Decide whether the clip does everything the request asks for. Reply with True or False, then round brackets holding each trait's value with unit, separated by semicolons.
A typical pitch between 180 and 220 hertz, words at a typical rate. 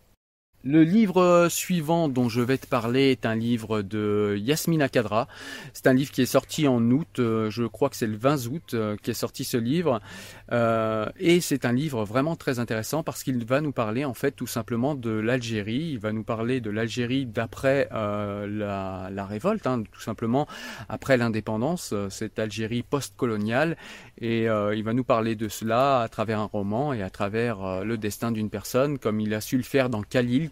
False (120 Hz; 195 wpm)